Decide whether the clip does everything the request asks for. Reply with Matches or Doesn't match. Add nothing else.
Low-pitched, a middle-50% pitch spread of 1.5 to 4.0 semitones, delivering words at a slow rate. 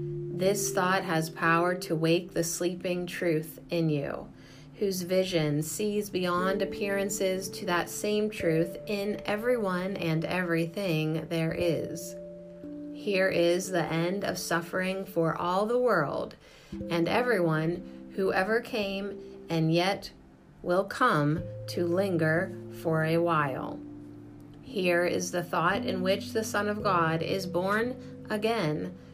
Doesn't match